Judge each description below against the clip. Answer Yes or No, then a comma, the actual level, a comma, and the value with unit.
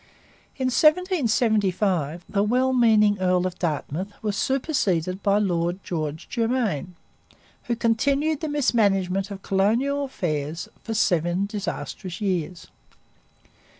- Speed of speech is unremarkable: No, slow, 110 wpm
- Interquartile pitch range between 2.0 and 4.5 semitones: No, average, 5.2 semitones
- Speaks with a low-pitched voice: No, high, 200 Hz